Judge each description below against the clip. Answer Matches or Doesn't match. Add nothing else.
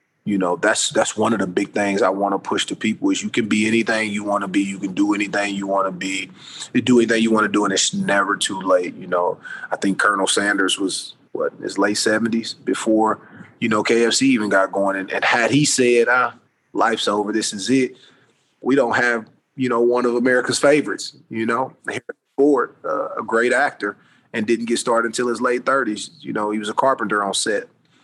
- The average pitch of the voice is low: Matches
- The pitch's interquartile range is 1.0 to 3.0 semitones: Doesn't match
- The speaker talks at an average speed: Doesn't match